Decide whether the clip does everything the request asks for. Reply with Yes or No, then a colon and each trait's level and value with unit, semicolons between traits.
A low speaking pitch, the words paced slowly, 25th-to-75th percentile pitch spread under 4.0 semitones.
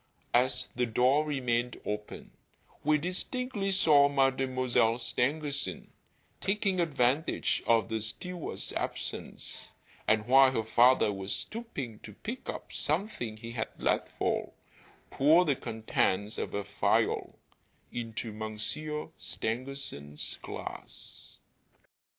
No: low, 130 Hz; slow, 110 wpm; average, 5.3 semitones